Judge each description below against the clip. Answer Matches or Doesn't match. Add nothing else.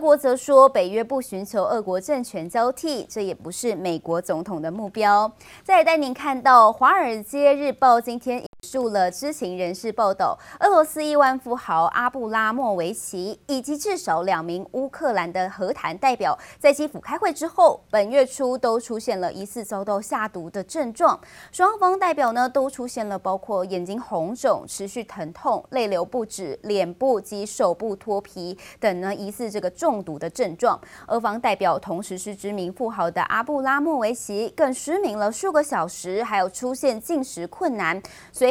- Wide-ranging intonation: Matches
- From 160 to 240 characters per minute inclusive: Doesn't match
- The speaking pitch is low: Doesn't match